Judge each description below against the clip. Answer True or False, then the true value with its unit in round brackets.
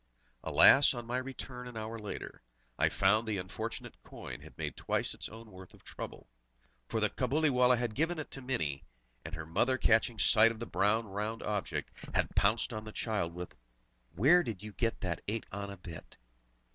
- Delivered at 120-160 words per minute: False (185 wpm)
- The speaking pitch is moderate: False (110 Hz)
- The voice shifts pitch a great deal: False (3.7 semitones)